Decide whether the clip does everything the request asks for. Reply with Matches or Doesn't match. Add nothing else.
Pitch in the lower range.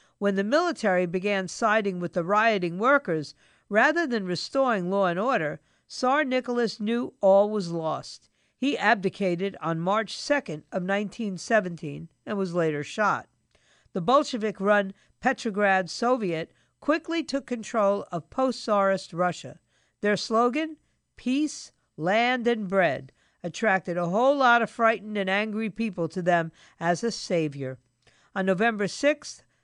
Doesn't match